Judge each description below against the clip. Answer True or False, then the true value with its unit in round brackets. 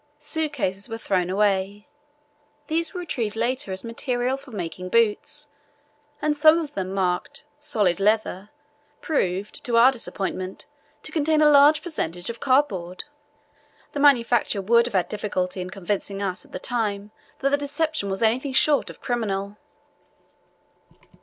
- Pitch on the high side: True (230 Hz)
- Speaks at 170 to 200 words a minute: False (145 wpm)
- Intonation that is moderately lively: False (6.7 semitones)